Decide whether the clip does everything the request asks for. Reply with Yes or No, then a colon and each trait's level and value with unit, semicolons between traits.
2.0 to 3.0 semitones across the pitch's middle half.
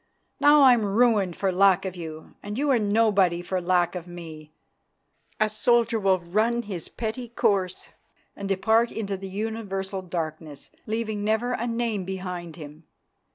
No: average, 3.9 semitones